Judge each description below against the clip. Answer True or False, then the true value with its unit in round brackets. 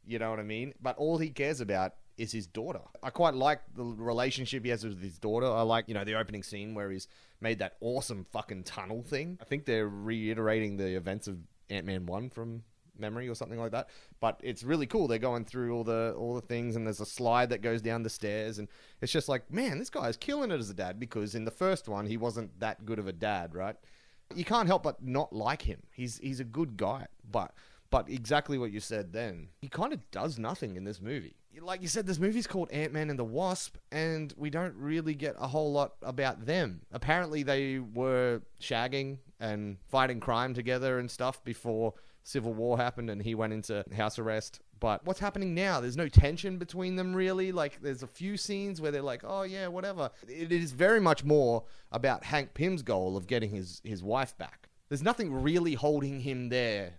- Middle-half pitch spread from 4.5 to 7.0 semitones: True (5.3 semitones)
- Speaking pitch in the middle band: False (120 Hz)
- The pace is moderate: False (220 wpm)